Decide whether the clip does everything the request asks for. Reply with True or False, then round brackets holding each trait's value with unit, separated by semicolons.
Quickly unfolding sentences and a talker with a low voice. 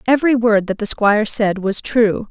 False (210 wpm; 220 Hz)